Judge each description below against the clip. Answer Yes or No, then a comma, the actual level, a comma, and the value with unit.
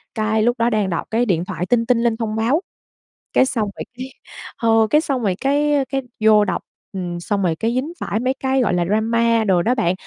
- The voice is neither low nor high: No, high, 225 Hz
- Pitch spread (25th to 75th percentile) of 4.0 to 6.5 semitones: No, average, 3.4 semitones